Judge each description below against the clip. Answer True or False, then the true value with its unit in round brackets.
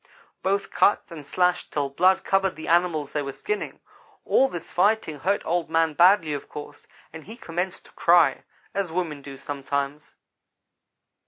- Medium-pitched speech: True (165 Hz)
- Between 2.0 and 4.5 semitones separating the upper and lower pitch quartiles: True (4.0 semitones)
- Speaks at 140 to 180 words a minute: True (160 wpm)